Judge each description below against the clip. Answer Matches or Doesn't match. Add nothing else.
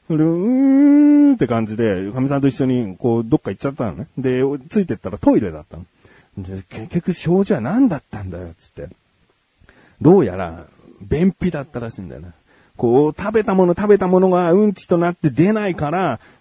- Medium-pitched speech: Matches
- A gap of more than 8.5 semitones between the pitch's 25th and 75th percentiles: Matches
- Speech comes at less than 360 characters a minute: Doesn't match